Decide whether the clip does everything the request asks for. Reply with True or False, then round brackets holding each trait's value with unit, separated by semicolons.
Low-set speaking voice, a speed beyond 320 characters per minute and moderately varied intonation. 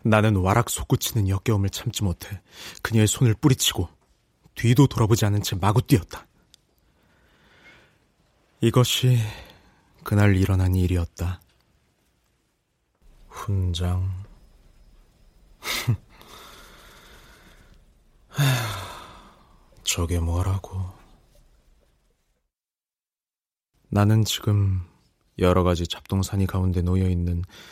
False (95 Hz; 170 characters per minute; 3.2 semitones)